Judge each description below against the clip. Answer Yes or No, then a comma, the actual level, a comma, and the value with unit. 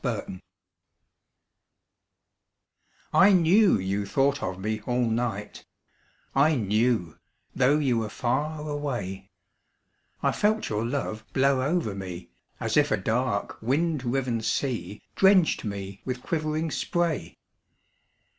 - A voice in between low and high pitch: No, low, 125 Hz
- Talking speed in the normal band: No, slow, 115 wpm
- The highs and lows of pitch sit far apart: Yes, wide, 6.1 semitones